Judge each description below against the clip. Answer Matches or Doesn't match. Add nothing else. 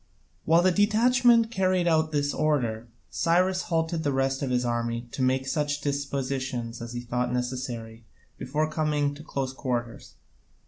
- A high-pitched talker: Doesn't match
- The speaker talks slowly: Doesn't match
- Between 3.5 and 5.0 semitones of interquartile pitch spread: Matches